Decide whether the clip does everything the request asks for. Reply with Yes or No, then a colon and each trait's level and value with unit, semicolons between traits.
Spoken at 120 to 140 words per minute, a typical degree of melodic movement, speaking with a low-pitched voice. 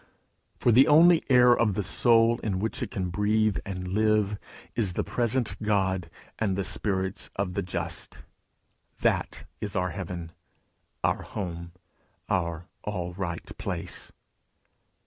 Yes: slow, 135 wpm; average, 3.3 semitones; low, 100 Hz